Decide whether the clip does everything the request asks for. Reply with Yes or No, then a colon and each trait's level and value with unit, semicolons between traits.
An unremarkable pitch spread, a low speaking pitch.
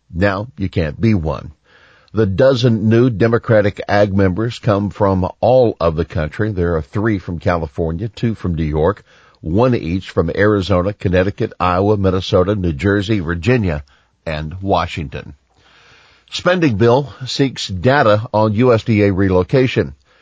Yes: average, 4.2 semitones; low, 100 Hz